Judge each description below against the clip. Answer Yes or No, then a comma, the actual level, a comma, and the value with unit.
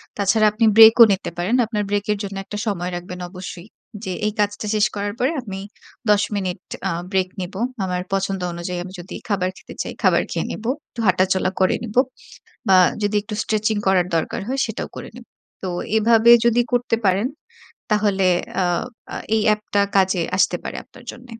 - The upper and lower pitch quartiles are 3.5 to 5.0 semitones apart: No, average, 2.7 semitones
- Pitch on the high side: Yes, high, 205 Hz